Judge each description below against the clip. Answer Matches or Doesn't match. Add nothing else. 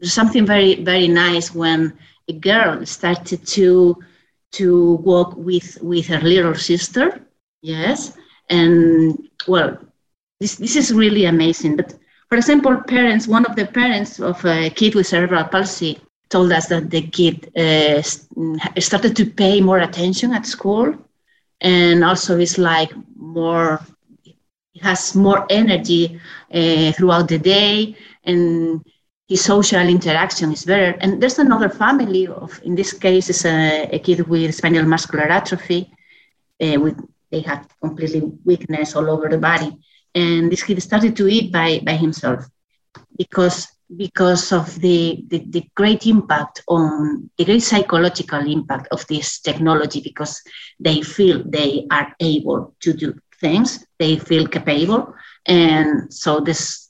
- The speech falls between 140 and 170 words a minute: Matches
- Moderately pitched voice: Matches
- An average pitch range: Matches